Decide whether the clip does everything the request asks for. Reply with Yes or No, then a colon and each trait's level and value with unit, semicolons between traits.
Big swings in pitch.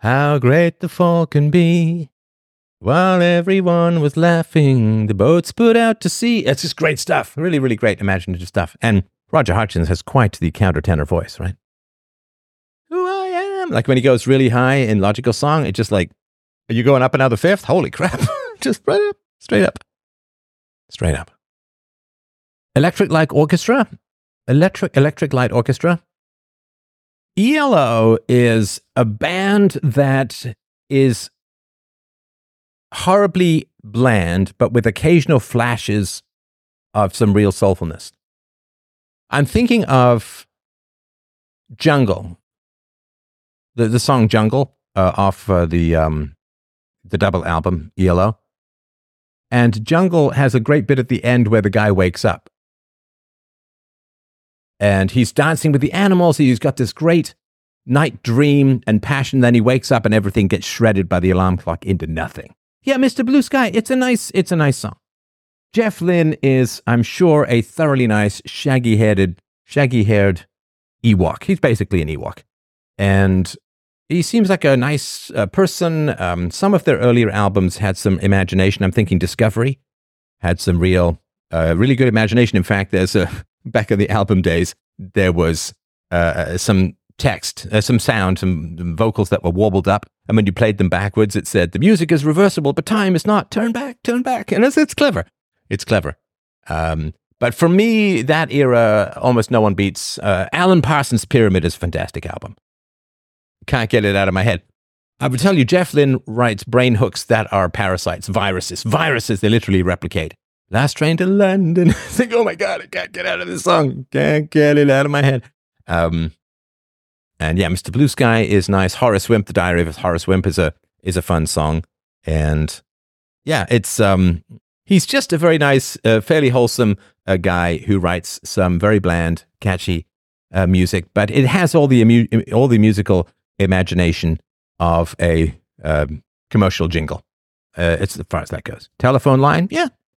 Yes: wide, 7.9 semitones